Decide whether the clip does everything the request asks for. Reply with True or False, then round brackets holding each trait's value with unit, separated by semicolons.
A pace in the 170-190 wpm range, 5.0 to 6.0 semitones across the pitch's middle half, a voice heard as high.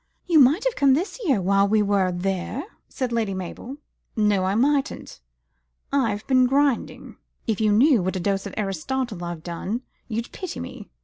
True (175 wpm; 5.5 semitones; 220 Hz)